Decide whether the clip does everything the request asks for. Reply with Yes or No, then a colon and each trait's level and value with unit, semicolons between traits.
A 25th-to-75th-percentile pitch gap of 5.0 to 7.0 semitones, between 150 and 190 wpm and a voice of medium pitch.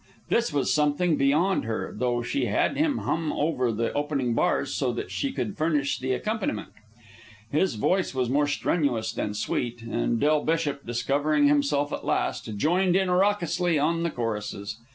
Yes: wide, 5.5 semitones; average, 165 wpm; medium, 145 Hz